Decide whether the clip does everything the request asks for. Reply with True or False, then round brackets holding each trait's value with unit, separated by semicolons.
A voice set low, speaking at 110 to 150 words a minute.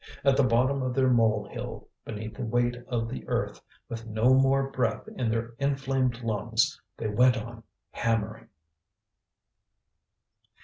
True (120 Hz; 140 wpm)